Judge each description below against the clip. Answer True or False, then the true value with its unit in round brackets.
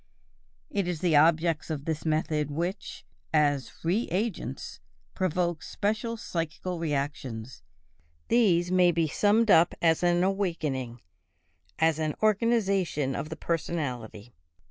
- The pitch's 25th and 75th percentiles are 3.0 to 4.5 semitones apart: True (3.7 semitones)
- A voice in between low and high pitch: True (165 Hz)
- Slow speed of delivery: True (120 wpm)